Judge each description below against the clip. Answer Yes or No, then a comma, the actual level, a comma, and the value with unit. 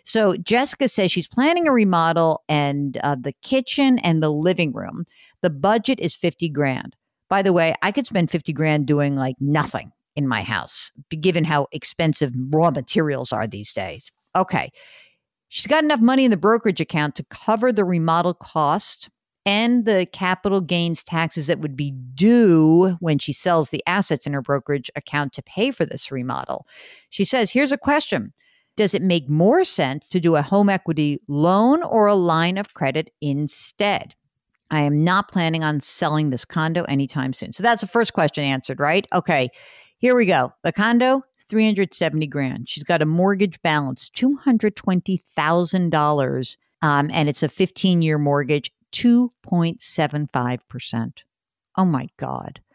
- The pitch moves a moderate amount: No, wide, 5.7 semitones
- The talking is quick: No, average, 175 wpm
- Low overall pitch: No, medium, 170 Hz